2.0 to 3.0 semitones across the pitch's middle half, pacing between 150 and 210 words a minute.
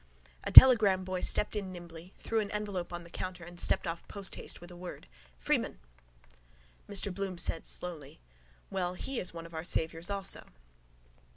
Yes: narrow, 2.5 semitones; average, 170 wpm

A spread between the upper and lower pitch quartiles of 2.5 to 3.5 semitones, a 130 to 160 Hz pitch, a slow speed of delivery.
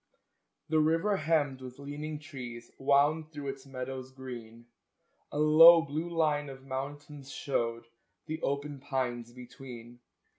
Yes: average, 2.9 semitones; medium, 140 Hz; slow, 125 wpm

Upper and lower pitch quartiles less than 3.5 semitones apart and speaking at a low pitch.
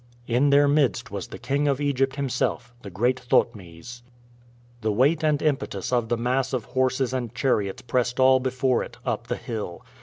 Yes: narrow, 2.4 semitones; low, 125 Hz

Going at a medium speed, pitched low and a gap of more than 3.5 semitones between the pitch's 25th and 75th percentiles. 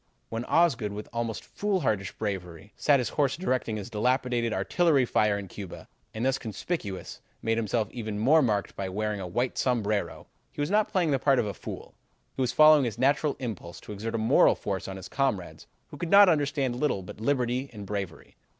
Yes: average, 195 wpm; low, 115 Hz; average, 5.1 semitones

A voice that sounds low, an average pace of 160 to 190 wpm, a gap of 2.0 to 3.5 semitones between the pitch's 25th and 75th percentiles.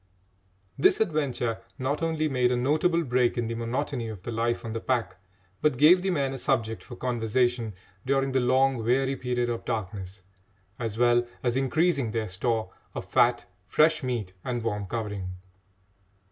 Yes: low, 125 Hz; average, 165 wpm; average, 3.1 semitones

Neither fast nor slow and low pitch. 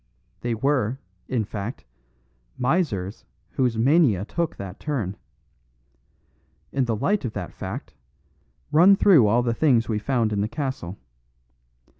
No: slow, 130 wpm; low, 120 Hz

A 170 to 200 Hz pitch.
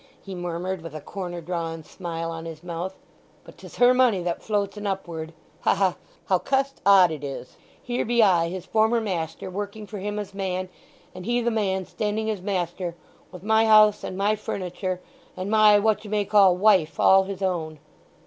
Yes: high, 190 Hz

